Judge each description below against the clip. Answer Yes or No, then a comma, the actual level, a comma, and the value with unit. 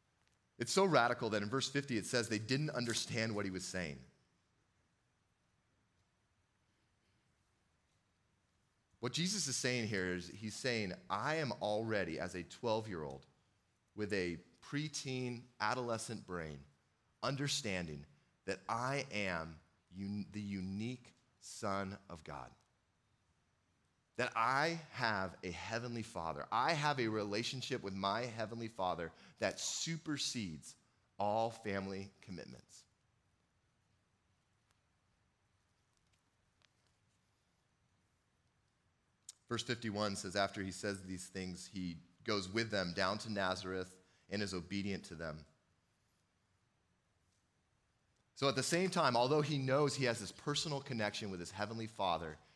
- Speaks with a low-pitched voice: Yes, low, 105 Hz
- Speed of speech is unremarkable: No, slow, 120 wpm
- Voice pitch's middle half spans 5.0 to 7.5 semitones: No, average, 4.3 semitones